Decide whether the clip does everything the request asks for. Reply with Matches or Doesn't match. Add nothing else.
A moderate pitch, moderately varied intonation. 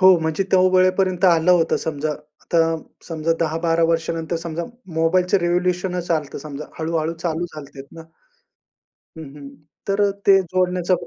Doesn't match